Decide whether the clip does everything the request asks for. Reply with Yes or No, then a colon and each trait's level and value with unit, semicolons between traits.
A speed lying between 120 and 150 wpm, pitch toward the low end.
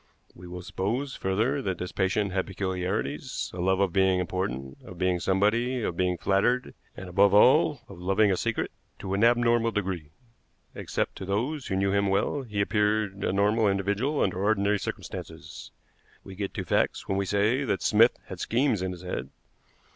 No: average, 180 wpm; low, 100 Hz